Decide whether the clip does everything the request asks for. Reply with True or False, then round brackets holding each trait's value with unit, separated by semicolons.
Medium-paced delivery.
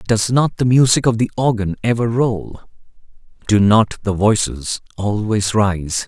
True (150 wpm)